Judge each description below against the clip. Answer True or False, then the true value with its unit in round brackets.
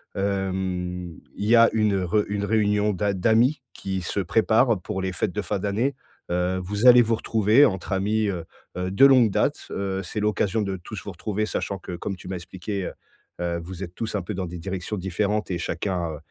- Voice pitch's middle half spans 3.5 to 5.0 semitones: False (2.7 semitones)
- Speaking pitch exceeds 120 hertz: False (100 Hz)